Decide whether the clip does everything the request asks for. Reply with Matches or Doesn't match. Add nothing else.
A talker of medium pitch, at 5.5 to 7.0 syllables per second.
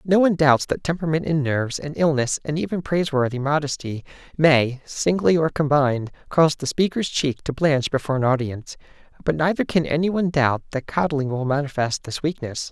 Matches